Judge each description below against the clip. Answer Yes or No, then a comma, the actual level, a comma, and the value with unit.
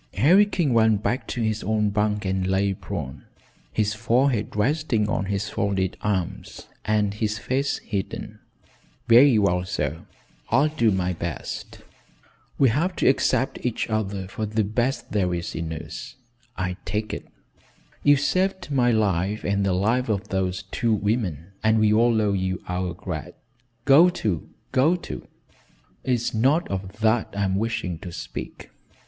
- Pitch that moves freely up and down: No, average, 4.1 semitones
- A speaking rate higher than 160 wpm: No, average, 155 wpm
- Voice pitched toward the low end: Yes, low, 105 Hz